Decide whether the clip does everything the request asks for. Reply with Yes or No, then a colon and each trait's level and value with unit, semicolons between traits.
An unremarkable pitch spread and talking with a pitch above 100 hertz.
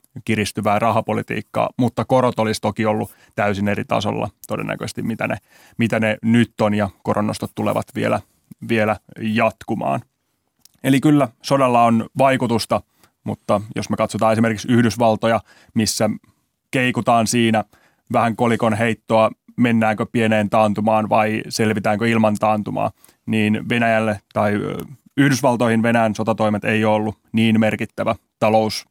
No: narrow, 1.4 semitones; low, 110 Hz